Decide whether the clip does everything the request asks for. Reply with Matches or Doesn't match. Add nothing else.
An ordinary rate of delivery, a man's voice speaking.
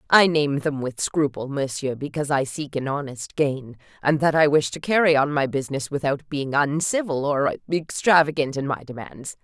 Doesn't match